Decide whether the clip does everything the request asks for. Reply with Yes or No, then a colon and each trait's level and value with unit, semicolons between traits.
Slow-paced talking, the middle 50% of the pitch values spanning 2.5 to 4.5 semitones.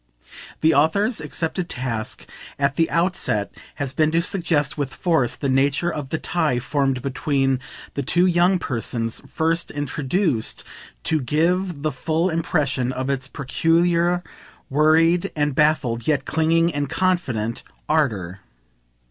Yes: slow, 130 wpm; average, 4.1 semitones